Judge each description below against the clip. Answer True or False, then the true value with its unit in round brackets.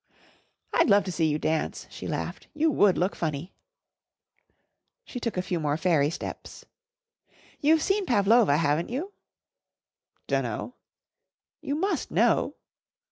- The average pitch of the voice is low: False (190 Hz)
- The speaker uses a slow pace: True (130 wpm)